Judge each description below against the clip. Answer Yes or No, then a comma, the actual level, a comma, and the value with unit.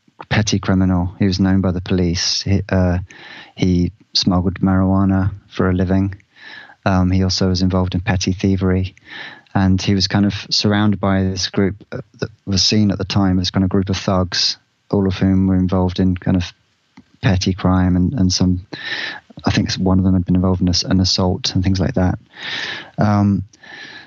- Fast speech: No, average, 185 wpm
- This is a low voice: Yes, very low, 95 Hz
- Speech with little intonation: Yes, narrow, 1.0 semitones